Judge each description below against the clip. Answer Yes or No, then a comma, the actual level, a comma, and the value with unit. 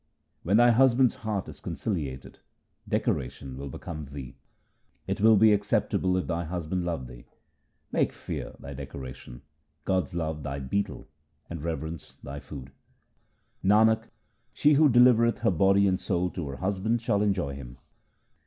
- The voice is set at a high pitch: No, very low, 90 Hz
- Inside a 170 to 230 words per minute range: No, average, 145 wpm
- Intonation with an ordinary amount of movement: No, wide, 7.2 semitones